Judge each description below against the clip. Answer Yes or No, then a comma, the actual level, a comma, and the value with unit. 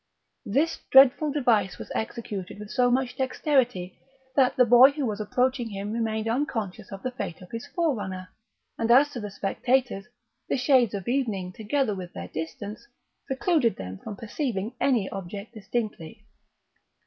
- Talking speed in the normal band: Yes, average, 155 wpm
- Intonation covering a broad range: No, average, 4.6 semitones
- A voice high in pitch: Yes, high, 225 Hz